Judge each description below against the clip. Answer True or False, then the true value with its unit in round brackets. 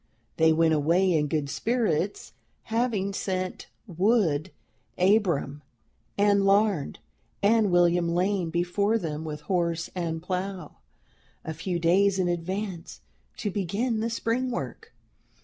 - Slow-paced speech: True (120 wpm)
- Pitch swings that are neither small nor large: True (3.8 semitones)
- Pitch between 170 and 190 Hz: True (185 Hz)